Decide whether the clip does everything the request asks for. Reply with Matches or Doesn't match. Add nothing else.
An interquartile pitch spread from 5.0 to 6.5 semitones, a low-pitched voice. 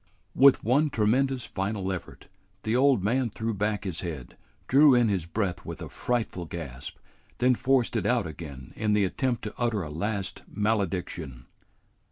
Matches